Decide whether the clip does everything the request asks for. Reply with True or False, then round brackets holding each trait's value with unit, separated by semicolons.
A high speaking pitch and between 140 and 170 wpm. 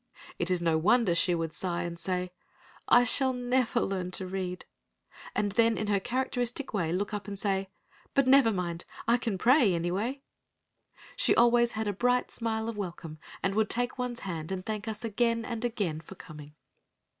False (205 Hz; 185 wpm)